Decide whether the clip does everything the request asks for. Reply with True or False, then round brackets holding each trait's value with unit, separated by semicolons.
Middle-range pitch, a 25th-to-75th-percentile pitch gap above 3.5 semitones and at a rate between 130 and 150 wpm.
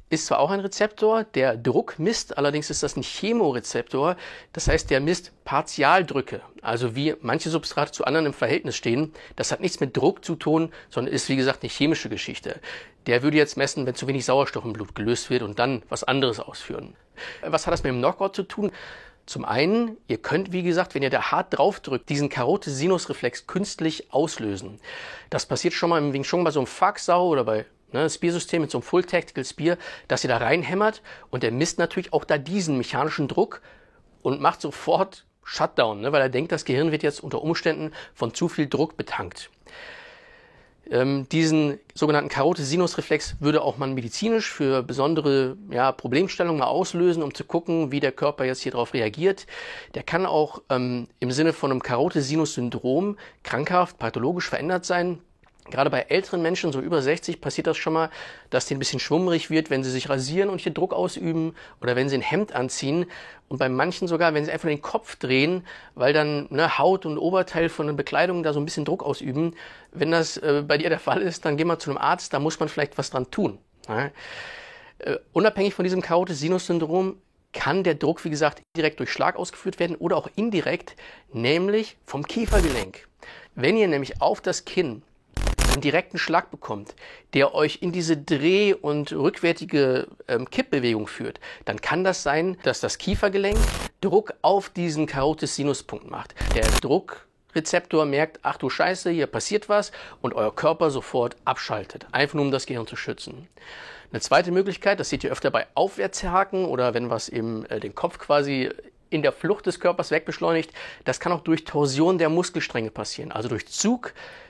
False (160 Hz; 4.4 semitones; 185 wpm)